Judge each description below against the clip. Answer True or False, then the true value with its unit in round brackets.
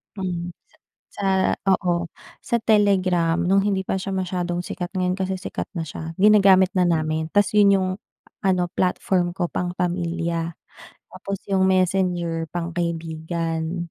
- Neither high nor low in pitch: True (180 Hz)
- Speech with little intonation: True (2.0 semitones)